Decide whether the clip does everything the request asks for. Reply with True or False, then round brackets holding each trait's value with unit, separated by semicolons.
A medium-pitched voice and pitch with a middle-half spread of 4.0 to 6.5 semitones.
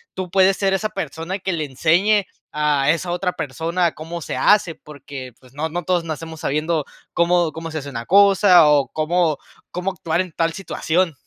False (165 Hz; 3.1 semitones)